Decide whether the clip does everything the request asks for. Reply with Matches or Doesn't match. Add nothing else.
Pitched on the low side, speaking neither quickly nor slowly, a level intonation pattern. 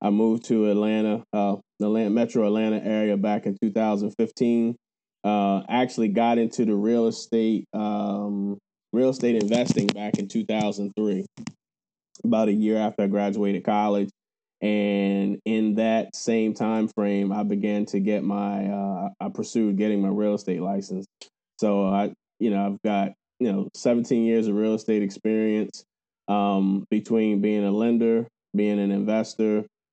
Matches